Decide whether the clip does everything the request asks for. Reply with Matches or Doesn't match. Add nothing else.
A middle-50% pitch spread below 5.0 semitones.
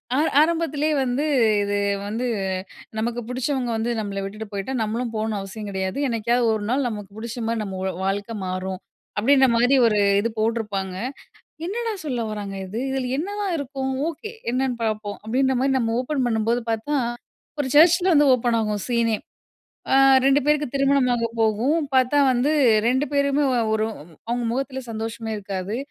Matches